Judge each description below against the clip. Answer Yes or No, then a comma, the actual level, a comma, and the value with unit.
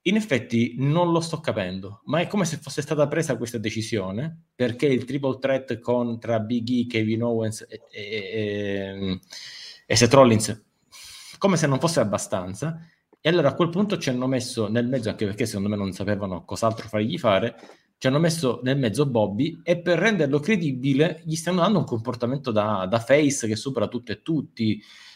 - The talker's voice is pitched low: Yes, low, 125 Hz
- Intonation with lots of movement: Yes, wide, 5.7 semitones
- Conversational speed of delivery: No, fast, 185 wpm